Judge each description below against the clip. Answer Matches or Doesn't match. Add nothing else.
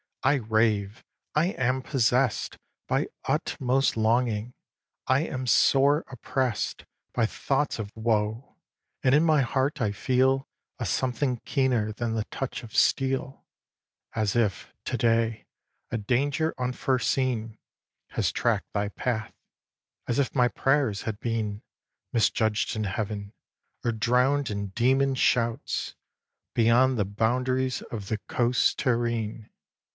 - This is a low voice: Matches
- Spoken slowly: Matches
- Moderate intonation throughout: Matches